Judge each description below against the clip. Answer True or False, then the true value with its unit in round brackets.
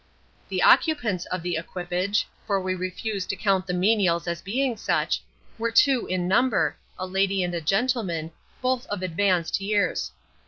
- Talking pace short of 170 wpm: True (155 wpm)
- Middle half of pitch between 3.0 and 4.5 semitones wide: True (3.5 semitones)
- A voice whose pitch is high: True (195 Hz)